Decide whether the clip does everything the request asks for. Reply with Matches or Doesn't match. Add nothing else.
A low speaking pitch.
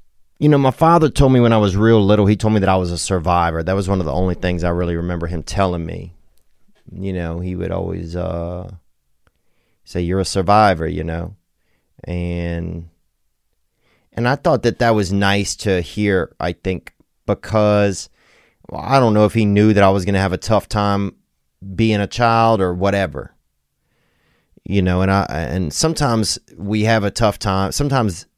Matches